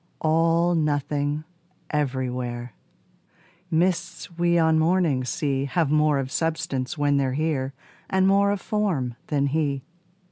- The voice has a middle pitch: Yes, medium, 150 Hz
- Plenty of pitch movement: No, average, 3.6 semitones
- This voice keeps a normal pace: No, slow, 120 wpm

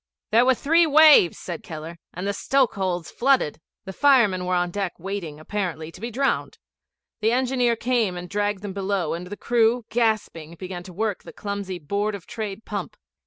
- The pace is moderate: Yes, average, 180 wpm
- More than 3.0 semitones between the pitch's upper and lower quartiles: Yes, average, 4.7 semitones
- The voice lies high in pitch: Yes, high, 200 Hz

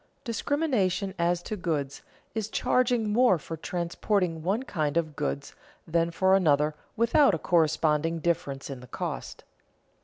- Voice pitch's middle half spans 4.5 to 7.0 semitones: Yes, average, 5.1 semitones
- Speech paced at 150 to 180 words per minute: No, average, 140 wpm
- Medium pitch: Yes, medium, 170 Hz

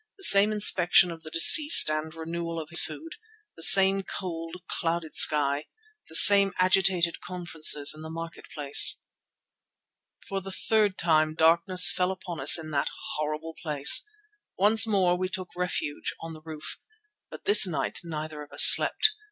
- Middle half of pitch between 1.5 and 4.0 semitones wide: Yes, average, 3.2 semitones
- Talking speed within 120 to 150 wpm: No, average, 160 wpm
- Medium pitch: Yes, medium, 170 Hz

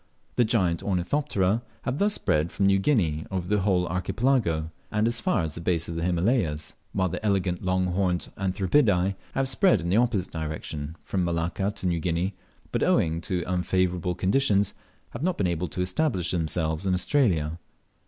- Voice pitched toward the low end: Yes, very low, 90 Hz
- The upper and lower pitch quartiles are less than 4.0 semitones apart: Yes, average, 3.3 semitones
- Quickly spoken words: No, average, 175 wpm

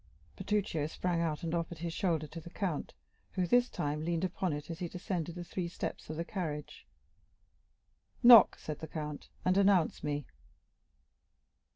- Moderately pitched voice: Yes, medium, 170 Hz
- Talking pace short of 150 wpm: No, average, 165 wpm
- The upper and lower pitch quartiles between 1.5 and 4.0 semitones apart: Yes, average, 2.9 semitones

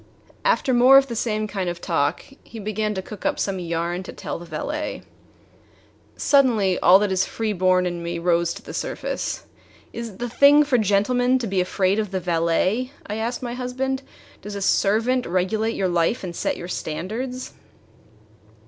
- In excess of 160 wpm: Yes, average, 185 wpm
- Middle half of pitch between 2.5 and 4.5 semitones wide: No, average, 5.3 semitones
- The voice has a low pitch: No, high, 205 Hz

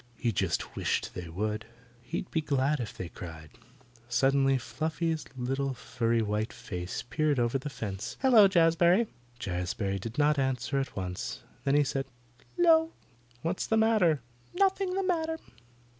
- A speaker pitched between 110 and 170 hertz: Yes, low, 135 Hz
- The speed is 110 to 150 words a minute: Yes, average, 145 wpm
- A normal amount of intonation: No, wide, 7.7 semitones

